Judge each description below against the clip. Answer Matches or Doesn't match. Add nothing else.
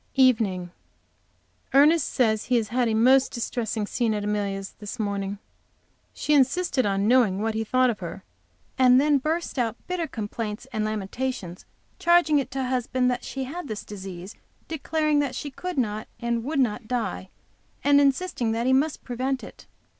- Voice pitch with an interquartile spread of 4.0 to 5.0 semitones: Matches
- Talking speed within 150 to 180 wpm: Matches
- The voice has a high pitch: Matches